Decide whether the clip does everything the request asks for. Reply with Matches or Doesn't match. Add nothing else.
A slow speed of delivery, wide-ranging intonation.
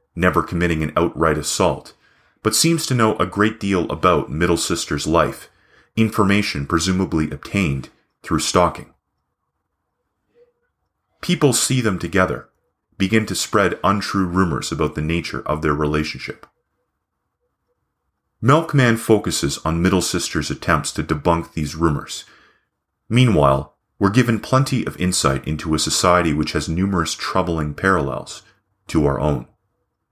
Matches